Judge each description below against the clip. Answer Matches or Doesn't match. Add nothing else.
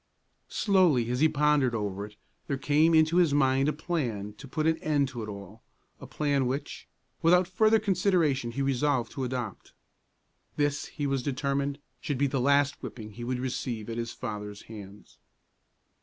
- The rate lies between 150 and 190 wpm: Matches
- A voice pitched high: Doesn't match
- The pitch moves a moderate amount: Matches